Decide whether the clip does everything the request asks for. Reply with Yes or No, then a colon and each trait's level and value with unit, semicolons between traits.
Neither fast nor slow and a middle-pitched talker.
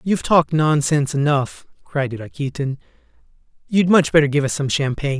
Yes: average, 150 wpm; medium, 145 Hz